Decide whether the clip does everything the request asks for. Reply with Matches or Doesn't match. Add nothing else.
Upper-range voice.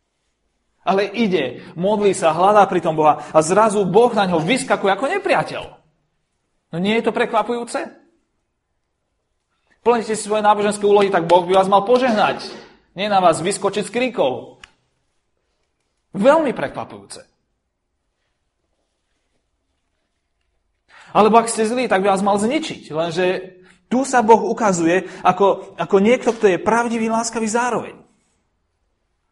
Matches